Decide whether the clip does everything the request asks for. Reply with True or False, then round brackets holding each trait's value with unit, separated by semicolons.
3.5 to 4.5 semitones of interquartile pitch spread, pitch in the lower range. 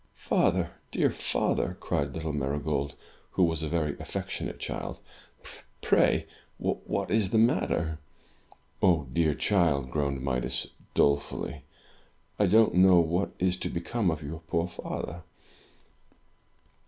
True (3.9 semitones; 80 Hz)